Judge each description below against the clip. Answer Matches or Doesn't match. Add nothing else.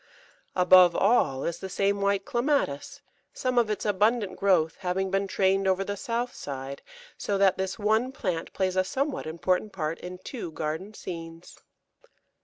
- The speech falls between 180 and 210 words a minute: Doesn't match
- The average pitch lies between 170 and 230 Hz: Matches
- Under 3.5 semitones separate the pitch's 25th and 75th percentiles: Matches